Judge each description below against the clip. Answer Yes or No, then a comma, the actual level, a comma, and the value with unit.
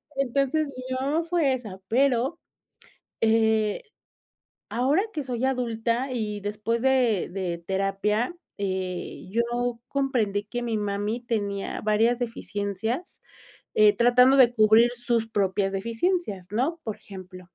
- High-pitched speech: Yes, high, 230 Hz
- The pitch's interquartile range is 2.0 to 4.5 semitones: Yes, average, 3.7 semitones